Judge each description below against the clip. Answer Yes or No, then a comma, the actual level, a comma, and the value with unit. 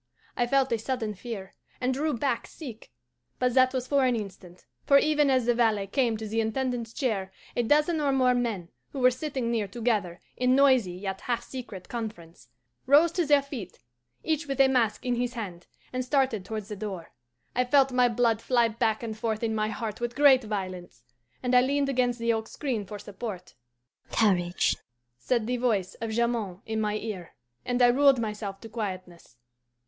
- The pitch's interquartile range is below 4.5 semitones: Yes, average, 3.5 semitones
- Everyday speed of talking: Yes, average, 190 wpm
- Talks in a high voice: Yes, high, 235 Hz